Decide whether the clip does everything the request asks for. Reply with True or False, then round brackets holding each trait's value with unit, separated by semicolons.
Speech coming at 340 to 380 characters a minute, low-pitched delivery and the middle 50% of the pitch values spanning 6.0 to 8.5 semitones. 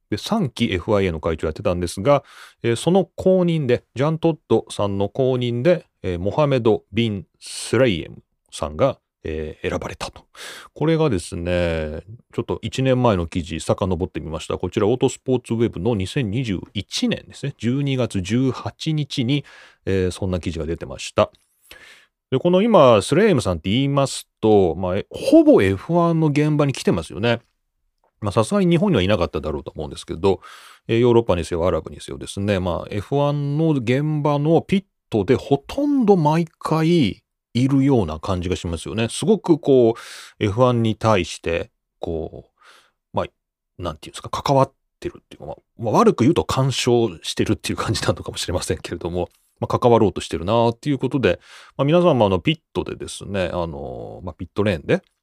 True (355 characters per minute; 120 Hz; 7.4 semitones)